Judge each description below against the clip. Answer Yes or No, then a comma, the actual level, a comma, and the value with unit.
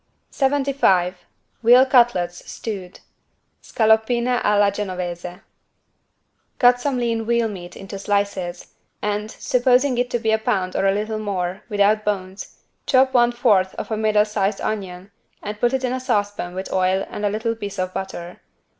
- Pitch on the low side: No, high, 210 Hz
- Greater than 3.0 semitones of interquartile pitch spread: Yes, average, 4.0 semitones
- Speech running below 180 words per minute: Yes, average, 155 wpm